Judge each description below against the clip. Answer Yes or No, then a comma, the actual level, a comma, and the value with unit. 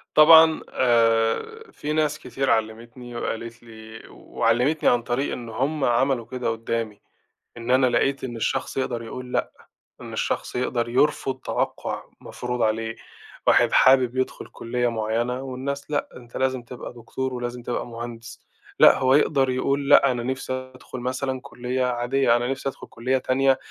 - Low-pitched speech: Yes, low, 125 Hz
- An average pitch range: No, narrow, 2.1 semitones